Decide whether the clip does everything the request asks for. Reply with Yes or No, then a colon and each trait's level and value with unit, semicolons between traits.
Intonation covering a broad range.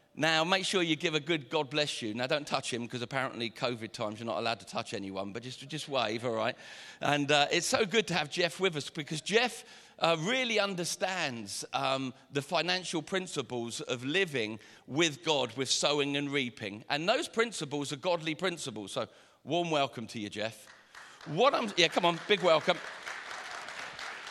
Yes: wide, 5.8 semitones